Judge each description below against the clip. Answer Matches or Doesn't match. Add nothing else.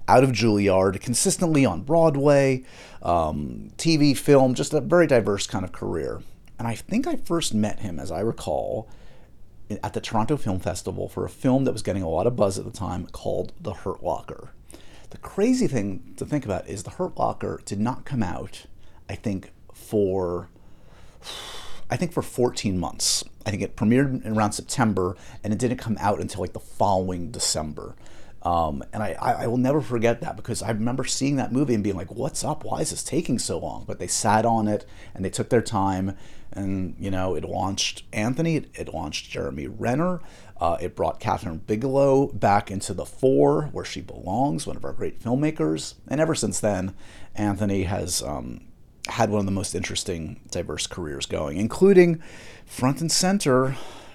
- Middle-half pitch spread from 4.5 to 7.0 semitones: Matches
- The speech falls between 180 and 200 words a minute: Matches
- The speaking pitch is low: Matches